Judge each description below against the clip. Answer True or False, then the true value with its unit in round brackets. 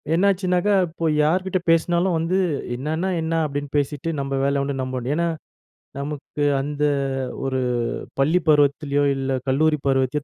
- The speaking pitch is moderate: True (150 Hz)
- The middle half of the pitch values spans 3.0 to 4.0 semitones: True (3.4 semitones)